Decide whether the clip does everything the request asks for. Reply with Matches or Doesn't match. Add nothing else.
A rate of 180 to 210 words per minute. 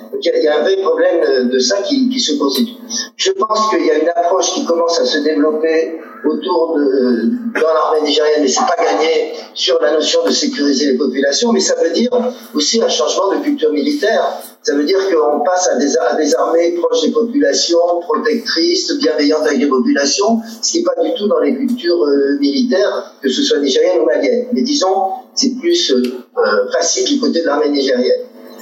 Matches